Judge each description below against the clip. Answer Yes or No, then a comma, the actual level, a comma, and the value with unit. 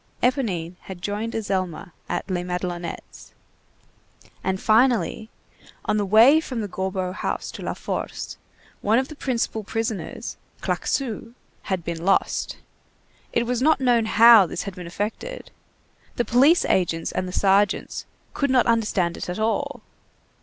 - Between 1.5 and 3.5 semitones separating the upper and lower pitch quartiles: No, average, 4.4 semitones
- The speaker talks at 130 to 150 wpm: Yes, average, 145 wpm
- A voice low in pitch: No, high, 210 Hz